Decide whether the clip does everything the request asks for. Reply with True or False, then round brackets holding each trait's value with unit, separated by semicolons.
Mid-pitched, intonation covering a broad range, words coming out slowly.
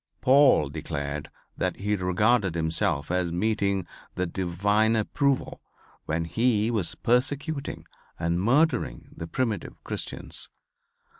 False (100 Hz; 6.0 semitones; 105 wpm)